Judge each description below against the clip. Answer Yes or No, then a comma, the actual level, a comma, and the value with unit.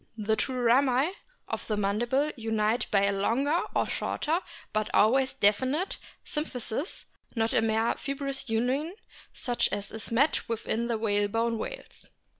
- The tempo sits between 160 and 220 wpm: No, average, 145 wpm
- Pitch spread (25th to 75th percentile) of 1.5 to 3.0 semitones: No, average, 3.8 semitones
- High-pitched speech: Yes, high, 235 Hz